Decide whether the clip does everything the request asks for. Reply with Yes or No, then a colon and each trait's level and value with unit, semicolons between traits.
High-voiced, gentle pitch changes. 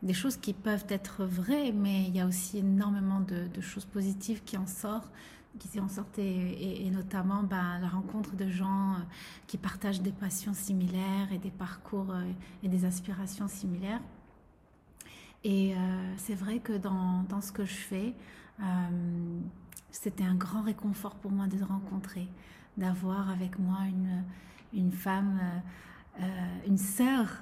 Yes: high, 195 Hz; narrow, 1.5 semitones